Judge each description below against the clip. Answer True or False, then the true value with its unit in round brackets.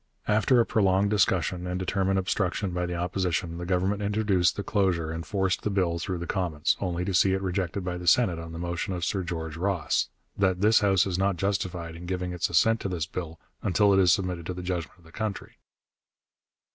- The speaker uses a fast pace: True (215 wpm)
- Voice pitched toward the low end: True (90 Hz)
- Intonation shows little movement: True (2.1 semitones)